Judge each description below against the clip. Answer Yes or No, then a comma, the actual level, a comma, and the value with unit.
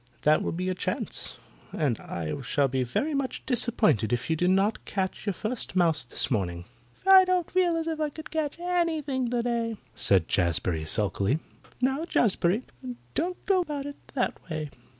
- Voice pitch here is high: Yes, high, 220 Hz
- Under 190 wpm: Yes, average, 170 wpm